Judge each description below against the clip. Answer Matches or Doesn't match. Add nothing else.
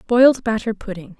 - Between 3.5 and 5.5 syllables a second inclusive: Doesn't match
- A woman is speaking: Matches